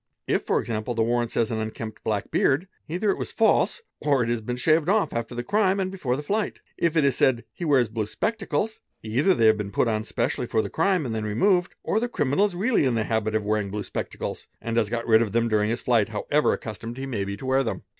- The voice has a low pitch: Yes, low, 120 Hz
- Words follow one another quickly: Yes, fast, 265 wpm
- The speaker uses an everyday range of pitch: No, wide, 7.0 semitones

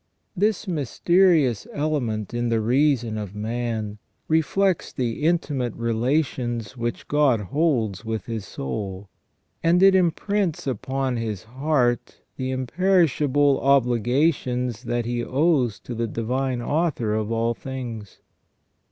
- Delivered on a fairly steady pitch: No, average, 4.6 semitones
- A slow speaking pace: Yes, slow, 120 wpm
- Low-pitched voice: Yes, low, 125 Hz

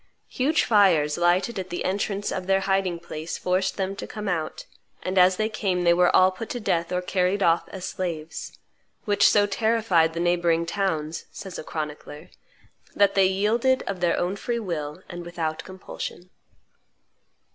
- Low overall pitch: No, medium, 185 Hz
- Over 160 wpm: Yes, average, 170 wpm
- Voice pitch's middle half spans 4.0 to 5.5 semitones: No, average, 2.7 semitones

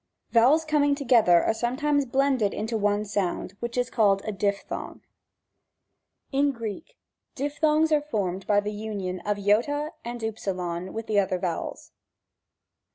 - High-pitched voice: Yes, high, 225 Hz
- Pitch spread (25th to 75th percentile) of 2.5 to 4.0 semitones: No, wide, 5.5 semitones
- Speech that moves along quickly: No, average, 145 wpm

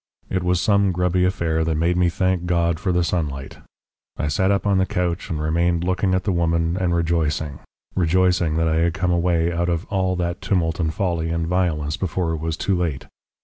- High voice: No, very low, 85 Hz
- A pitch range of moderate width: No, narrow, 2.0 semitones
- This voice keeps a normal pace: No, fast, 210 wpm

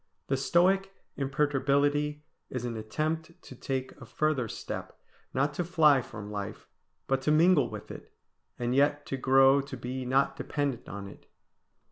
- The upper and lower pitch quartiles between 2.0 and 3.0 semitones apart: Yes, narrow, 2.6 semitones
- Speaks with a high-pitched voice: No, low, 135 Hz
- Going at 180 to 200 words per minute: No, average, 155 wpm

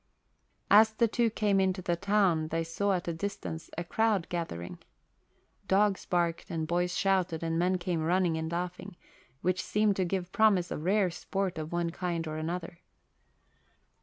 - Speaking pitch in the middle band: Yes, medium, 180 Hz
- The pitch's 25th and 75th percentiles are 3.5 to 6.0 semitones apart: No, average, 2.8 semitones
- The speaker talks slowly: No, average, 165 wpm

